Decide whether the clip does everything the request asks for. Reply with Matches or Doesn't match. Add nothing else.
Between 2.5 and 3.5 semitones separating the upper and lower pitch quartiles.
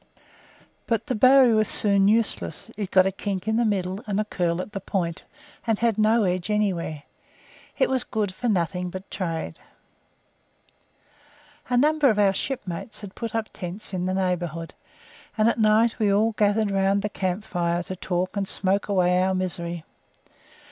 Matches